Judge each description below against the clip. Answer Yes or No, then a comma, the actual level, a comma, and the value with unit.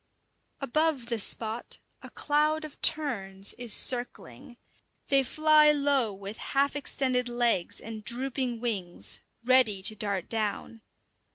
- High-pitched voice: Yes, high, 240 Hz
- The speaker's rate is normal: No, slow, 120 wpm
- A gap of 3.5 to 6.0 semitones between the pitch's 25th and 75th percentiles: Yes, average, 4.5 semitones